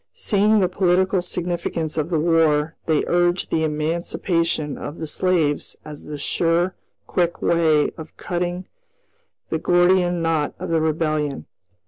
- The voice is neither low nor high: Yes, medium, 165 Hz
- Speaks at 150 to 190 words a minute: No, slow, 135 wpm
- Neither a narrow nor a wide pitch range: No, narrow, 2.3 semitones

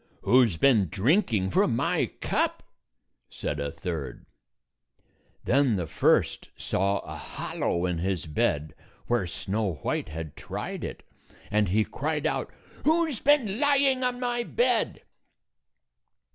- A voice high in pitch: No, low, 105 Hz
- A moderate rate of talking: No, slow, 130 wpm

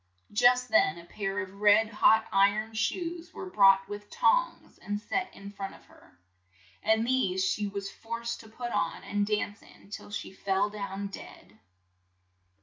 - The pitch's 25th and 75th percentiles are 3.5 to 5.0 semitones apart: No, average, 2.8 semitones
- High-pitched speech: Yes, high, 205 Hz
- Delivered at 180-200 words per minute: No, average, 165 wpm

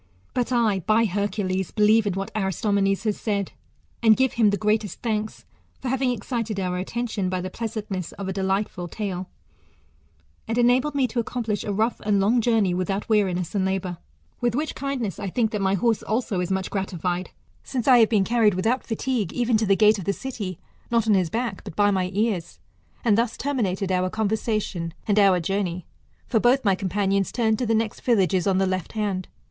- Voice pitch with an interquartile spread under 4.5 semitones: Yes, average, 3.2 semitones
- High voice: Yes, high, 210 Hz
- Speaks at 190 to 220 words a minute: Yes, average, 200 wpm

